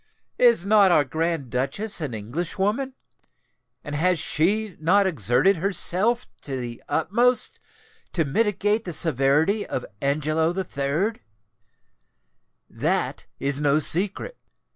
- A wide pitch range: Yes, wide, 6.2 semitones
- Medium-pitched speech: Yes, medium, 170 Hz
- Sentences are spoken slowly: Yes, slow, 110 wpm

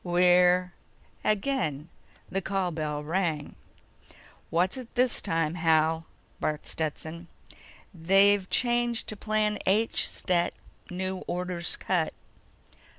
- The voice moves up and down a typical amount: Yes, average, 3.3 semitones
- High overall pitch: No, medium, 180 Hz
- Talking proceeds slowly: Yes, slow, 105 wpm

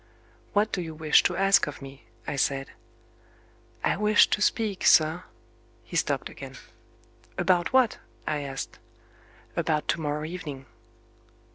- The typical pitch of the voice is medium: Yes, medium, 155 Hz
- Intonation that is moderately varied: Yes, average, 4.9 semitones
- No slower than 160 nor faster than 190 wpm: No, average, 140 wpm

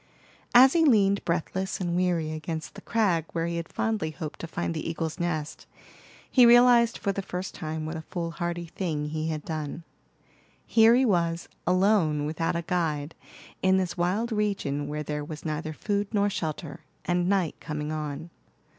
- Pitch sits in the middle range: Yes, medium, 170 Hz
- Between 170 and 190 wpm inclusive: Yes, average, 175 wpm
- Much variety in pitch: No, average, 3.9 semitones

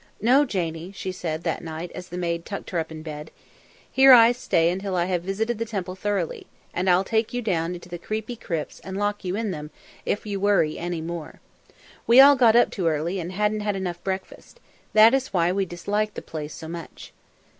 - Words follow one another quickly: Yes, fast, 215 wpm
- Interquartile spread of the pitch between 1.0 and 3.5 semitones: No, average, 3.9 semitones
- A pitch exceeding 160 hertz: Yes, medium, 185 Hz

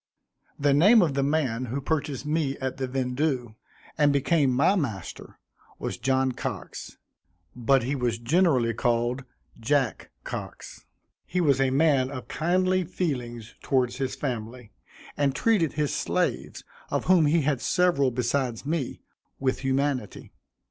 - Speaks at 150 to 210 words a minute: No, average, 140 wpm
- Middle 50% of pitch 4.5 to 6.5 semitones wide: No, average, 3.4 semitones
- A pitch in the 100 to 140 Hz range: Yes, low, 135 Hz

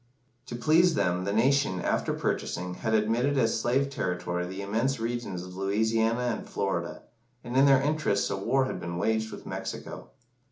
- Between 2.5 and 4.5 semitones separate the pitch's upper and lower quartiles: No, average, 5.2 semitones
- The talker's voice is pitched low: Yes, low, 115 Hz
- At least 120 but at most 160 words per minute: No, average, 170 wpm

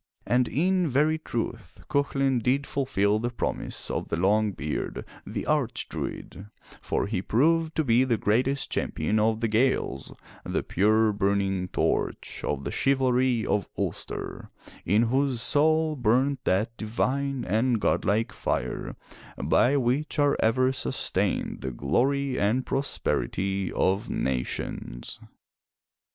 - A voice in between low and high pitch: No, low, 120 Hz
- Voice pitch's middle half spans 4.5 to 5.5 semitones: Yes, average, 5.1 semitones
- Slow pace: Yes, slow, 130 wpm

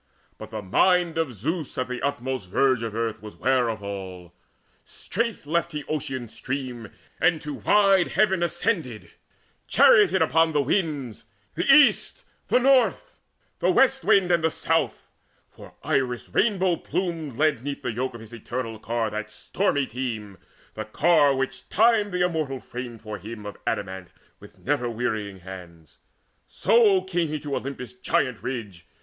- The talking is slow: No, average, 155 wpm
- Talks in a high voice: No, low, 135 Hz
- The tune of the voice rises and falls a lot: Yes, wide, 7.3 semitones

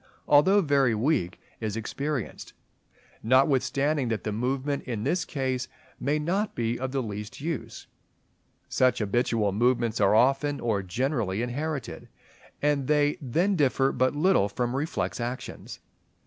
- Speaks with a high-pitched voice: No, low, 130 Hz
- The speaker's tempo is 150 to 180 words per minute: No, slow, 135 wpm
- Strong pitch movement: No, average, 4.1 semitones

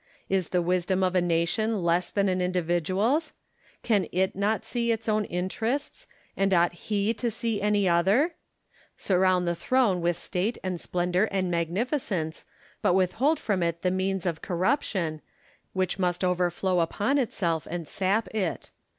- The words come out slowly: No, average, 160 wpm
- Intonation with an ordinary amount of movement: Yes, average, 3.4 semitones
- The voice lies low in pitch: No, medium, 185 Hz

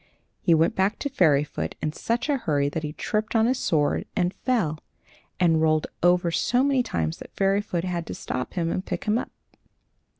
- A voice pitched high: No, medium, 175 Hz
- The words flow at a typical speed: Yes, average, 195 wpm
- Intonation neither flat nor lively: No, wide, 5.9 semitones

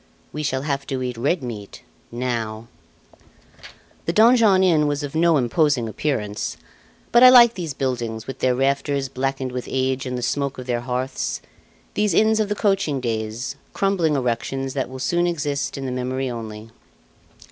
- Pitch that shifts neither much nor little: Yes, average, 4.1 semitones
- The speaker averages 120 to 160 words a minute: No, average, 170 wpm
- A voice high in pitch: No, low, 135 Hz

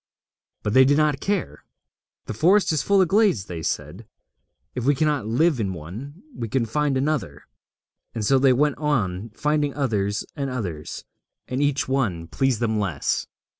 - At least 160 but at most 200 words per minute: Yes, average, 170 wpm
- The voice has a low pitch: Yes, low, 130 Hz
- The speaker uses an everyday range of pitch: No, wide, 6.0 semitones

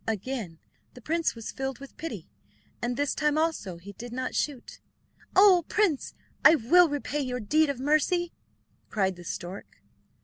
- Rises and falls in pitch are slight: No, wide, 5.5 semitones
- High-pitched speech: Yes, very high, 270 Hz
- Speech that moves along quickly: No, average, 160 wpm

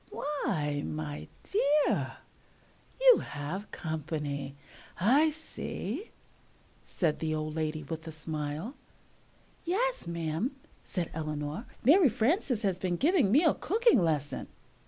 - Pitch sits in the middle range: Yes, medium, 170 Hz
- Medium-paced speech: No, slow, 115 wpm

